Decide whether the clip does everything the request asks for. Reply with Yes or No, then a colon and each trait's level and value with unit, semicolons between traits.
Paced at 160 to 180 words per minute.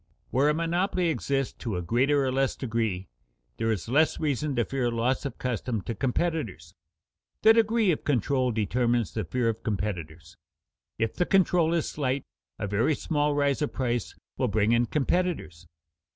Yes: average, 165 wpm